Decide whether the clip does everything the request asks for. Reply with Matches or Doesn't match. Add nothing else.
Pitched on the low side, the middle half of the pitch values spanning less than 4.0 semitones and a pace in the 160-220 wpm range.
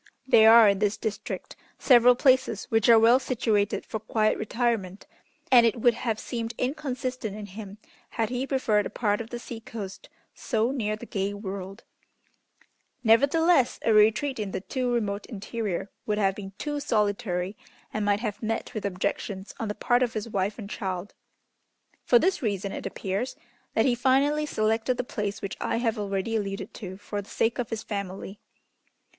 Doesn't match